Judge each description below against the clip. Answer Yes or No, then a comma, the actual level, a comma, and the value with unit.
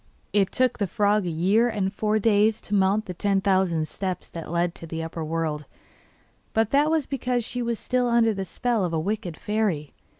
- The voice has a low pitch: No, high, 205 Hz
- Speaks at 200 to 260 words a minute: Yes, fast, 205 wpm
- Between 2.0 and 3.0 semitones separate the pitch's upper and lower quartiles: No, average, 4.5 semitones